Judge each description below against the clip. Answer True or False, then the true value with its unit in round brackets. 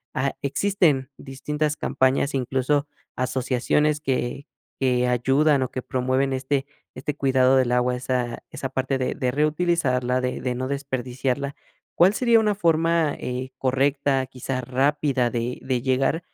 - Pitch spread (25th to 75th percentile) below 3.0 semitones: True (2.4 semitones)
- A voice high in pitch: False (135 Hz)